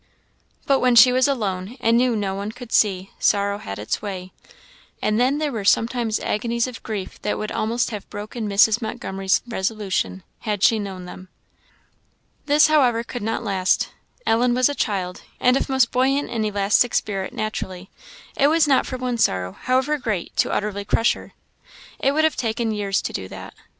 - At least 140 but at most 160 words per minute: No, average, 180 wpm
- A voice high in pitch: Yes, high, 220 Hz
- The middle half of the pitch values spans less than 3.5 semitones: No, average, 4.0 semitones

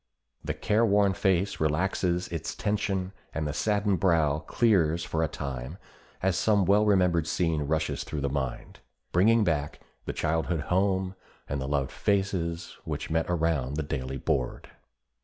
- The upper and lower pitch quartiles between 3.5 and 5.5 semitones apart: Yes, average, 4.3 semitones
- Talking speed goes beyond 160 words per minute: No, average, 155 wpm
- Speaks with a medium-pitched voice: No, very low, 85 Hz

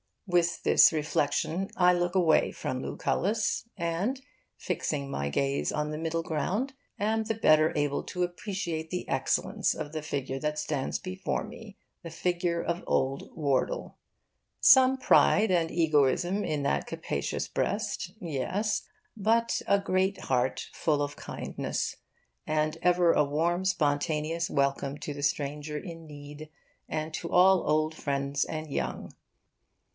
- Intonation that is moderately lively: Yes, average, 3.8 semitones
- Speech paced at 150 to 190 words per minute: No, average, 140 wpm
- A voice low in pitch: No, medium, 160 Hz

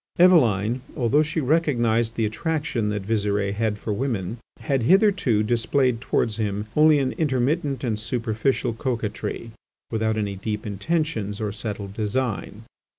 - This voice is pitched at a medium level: No, low, 115 Hz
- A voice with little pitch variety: No, average, 4.3 semitones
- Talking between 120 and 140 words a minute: Yes, slow, 135 wpm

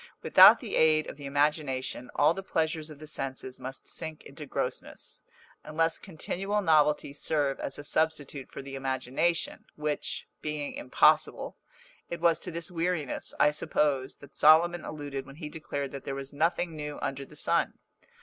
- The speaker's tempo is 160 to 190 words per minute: Yes, average, 165 wpm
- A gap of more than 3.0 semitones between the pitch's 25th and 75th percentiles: No, average, 2.7 semitones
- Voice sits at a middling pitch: Yes, medium, 150 Hz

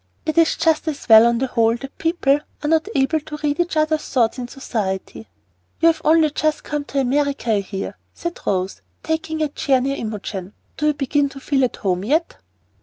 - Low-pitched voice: No, very high, 275 Hz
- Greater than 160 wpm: Yes, average, 200 wpm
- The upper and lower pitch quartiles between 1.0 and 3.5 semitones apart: No, average, 5.0 semitones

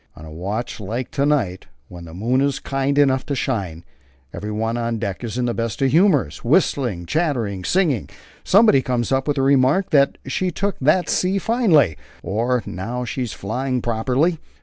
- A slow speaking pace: No, average, 180 wpm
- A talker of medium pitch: No, low, 125 Hz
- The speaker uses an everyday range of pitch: Yes, average, 4.7 semitones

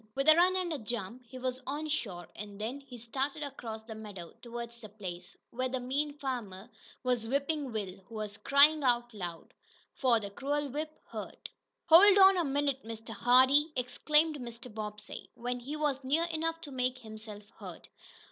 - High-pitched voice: Yes, very high, 255 Hz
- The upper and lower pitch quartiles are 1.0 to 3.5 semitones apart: No, average, 4.7 semitones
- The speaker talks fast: No, average, 180 wpm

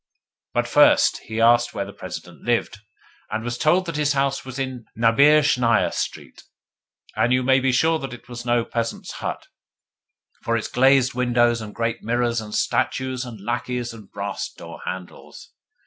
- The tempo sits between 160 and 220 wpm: Yes, average, 165 wpm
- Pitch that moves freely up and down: No, narrow, 2.4 semitones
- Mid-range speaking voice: No, low, 120 Hz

